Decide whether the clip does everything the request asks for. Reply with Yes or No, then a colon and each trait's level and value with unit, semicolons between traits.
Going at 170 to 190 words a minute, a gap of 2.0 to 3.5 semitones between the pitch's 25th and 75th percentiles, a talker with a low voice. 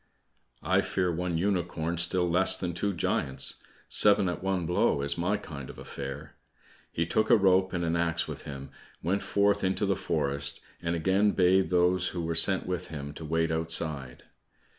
Yes: average, 180 wpm; average, 2.8 semitones; very low, 85 Hz